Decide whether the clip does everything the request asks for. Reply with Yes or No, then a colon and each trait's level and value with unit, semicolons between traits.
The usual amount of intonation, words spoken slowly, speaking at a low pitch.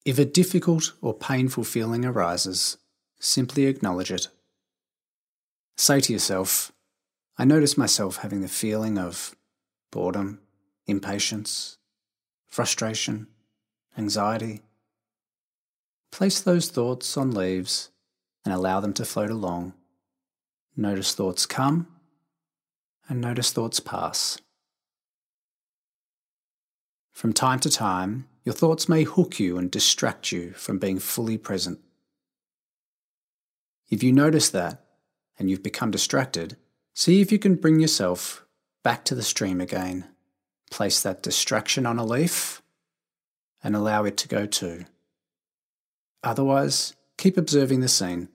No: wide, 6.1 semitones; slow, 115 wpm; low, 105 Hz